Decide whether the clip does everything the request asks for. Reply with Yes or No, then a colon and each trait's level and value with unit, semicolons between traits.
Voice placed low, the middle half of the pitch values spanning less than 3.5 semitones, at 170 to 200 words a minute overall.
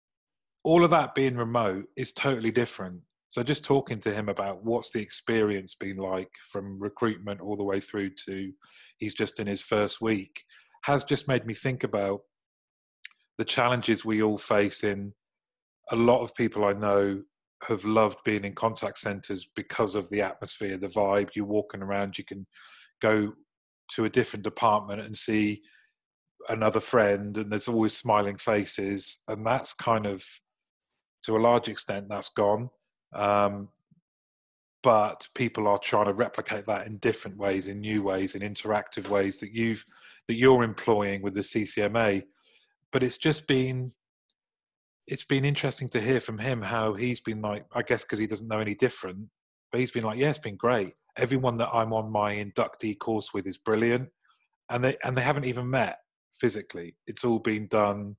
Yes: low, 110 Hz; average, 3.0 semitones; average, 175 wpm